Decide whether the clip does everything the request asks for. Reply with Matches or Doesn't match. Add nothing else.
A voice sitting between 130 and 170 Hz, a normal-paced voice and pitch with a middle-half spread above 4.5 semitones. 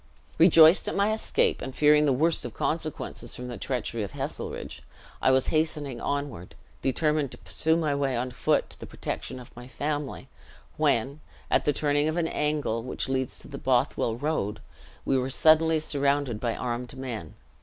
Doesn't match